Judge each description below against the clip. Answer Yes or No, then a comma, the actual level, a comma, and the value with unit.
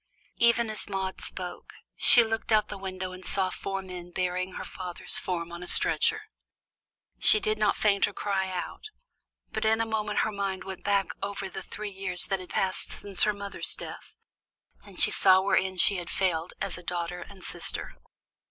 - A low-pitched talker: No, high, 190 Hz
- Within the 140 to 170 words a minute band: No, average, 190 wpm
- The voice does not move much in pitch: Yes, narrow, 2.0 semitones